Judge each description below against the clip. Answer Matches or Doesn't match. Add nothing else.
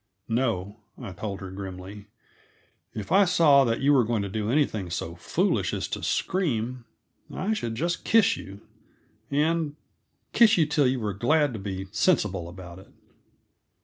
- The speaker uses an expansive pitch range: Matches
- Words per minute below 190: Matches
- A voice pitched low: Matches